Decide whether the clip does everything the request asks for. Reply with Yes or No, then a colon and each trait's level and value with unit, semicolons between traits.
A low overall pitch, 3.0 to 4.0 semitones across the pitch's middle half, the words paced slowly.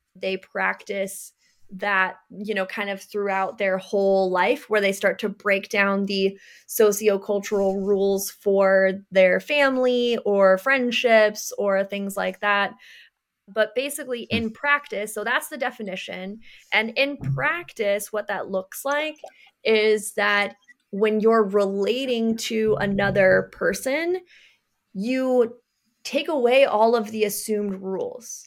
No: high, 210 Hz; average, 3.6 semitones; slow, 125 wpm